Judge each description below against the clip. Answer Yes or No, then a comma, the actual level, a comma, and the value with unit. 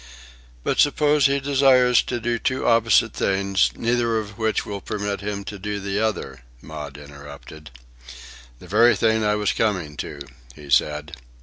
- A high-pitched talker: No, low, 105 Hz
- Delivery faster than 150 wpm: Yes, average, 160 wpm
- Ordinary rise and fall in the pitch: No, wide, 7.0 semitones